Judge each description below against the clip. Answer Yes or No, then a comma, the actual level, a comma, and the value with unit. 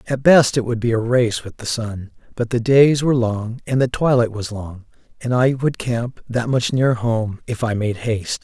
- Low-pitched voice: Yes, low, 120 Hz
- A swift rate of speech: Yes, fast, 230 wpm